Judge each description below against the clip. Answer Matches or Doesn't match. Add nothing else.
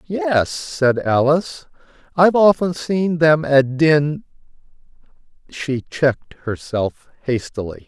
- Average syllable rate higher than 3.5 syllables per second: Doesn't match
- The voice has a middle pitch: Matches